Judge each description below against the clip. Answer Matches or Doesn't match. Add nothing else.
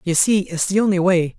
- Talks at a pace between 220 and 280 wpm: Matches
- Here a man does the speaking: Matches